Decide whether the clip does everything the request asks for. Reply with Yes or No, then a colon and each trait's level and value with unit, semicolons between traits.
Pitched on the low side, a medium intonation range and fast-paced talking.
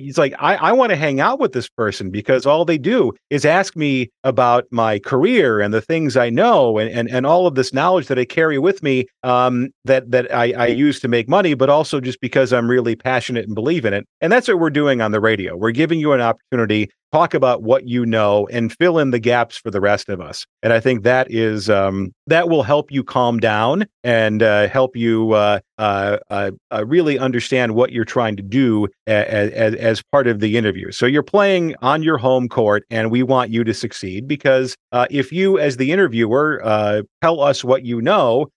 Yes: low, 125 Hz; average, 4.2 semitones; fast, 225 wpm